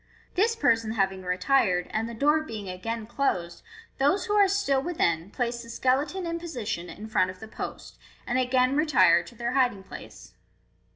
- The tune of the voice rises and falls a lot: Yes, wide, 6.7 semitones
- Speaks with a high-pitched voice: Yes, high, 235 Hz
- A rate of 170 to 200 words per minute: Yes, average, 175 wpm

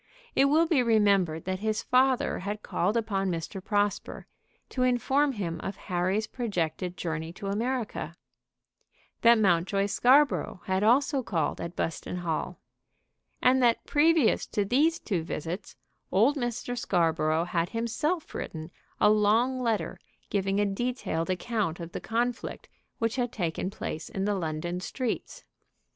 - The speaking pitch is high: Yes, high, 205 Hz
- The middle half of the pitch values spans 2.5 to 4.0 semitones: No, wide, 5.5 semitones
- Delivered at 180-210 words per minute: No, average, 140 wpm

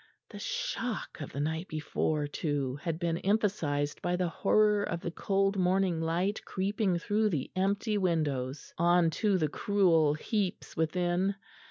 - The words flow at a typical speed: Yes, average, 150 wpm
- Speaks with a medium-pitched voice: Yes, medium, 175 Hz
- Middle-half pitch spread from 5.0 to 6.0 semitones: No, average, 4.2 semitones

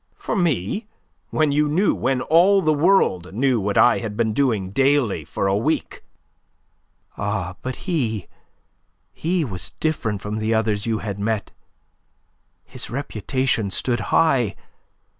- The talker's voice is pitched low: Yes, low, 120 Hz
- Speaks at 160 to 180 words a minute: No, average, 140 wpm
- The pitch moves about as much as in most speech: No, wide, 6.4 semitones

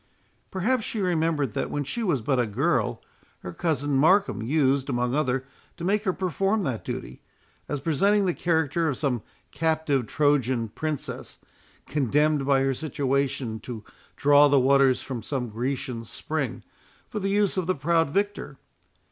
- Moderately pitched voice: Yes, medium, 145 Hz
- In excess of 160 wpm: No, average, 155 wpm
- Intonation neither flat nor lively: Yes, average, 4.4 semitones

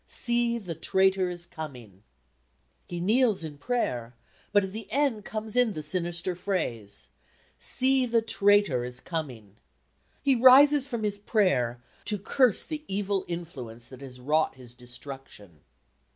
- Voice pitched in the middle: Yes, medium, 180 Hz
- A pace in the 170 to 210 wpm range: No, average, 140 wpm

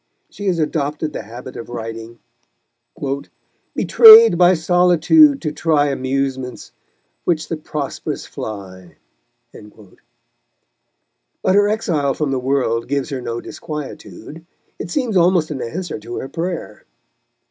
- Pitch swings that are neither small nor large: No, wide, 5.9 semitones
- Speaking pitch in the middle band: Yes, medium, 150 Hz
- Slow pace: Yes, slow, 120 wpm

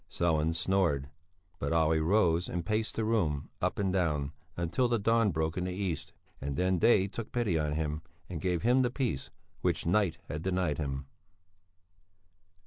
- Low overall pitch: Yes, very low, 85 Hz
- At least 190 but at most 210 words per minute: No, average, 165 wpm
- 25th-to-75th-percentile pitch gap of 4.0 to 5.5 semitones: Yes, average, 4.5 semitones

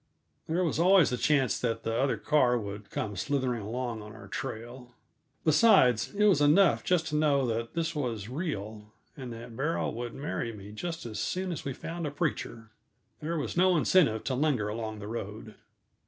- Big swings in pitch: Yes, wide, 5.7 semitones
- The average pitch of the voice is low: Yes, low, 130 Hz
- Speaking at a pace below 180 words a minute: No, average, 185 wpm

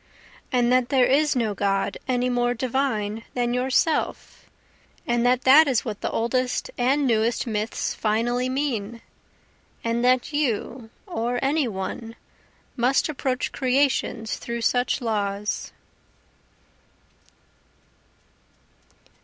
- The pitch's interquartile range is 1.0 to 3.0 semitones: Yes, narrow, 2.4 semitones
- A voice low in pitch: No, high, 245 Hz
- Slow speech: Yes, slow, 110 wpm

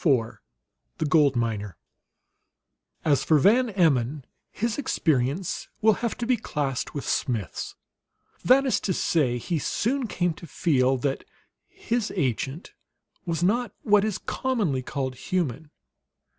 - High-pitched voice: No, medium, 160 Hz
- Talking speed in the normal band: No, slow, 130 wpm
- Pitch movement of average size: No, wide, 8.0 semitones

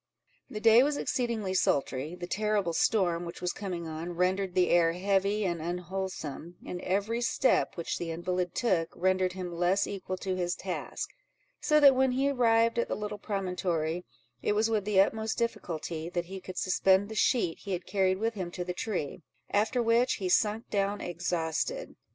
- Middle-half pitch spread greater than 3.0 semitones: Yes, average, 3.5 semitones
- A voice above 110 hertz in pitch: Yes, high, 190 Hz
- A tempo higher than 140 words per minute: Yes, average, 180 wpm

